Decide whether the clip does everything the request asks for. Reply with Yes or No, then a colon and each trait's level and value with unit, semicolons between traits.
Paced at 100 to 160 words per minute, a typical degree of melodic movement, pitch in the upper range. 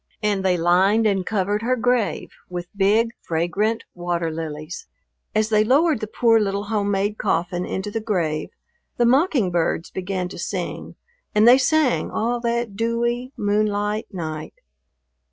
Yes: average, 145 wpm; average, 4.1 semitones; high, 205 Hz